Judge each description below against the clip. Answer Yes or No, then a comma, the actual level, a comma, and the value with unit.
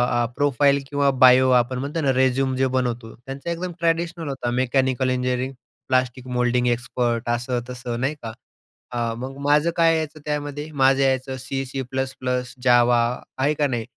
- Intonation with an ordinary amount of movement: No, narrow, 2.3 semitones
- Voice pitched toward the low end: Yes, low, 130 Hz